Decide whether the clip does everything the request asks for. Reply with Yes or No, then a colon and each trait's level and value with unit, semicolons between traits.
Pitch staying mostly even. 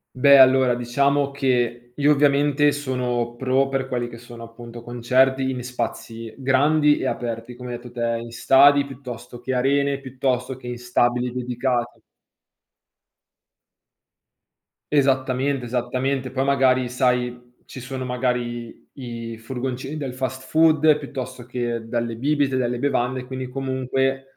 Yes: narrow, 1.9 semitones